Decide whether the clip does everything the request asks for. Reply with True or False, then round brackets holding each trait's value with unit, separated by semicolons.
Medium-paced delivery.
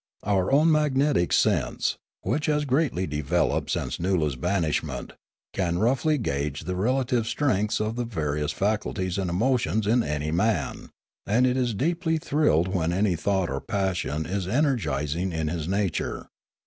True (155 wpm)